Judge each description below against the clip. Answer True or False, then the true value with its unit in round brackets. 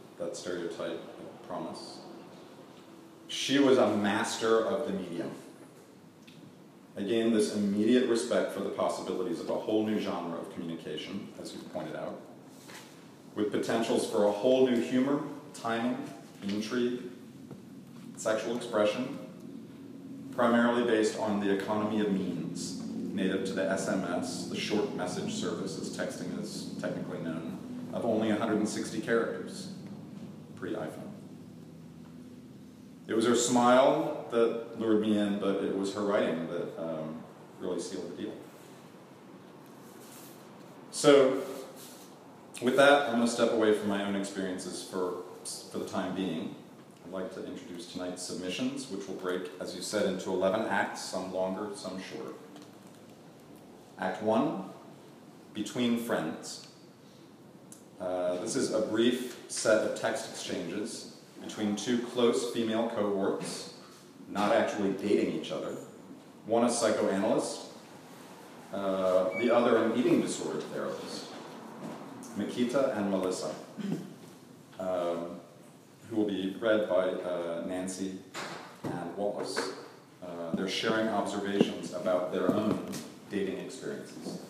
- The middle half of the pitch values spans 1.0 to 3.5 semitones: False (3.9 semitones)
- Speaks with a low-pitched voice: True (105 Hz)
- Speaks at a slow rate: True (125 wpm)